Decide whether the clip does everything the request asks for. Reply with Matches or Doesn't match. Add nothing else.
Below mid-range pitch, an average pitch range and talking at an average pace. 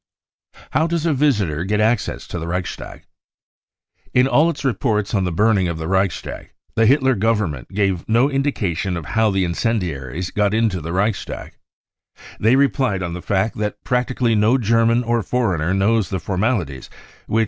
Matches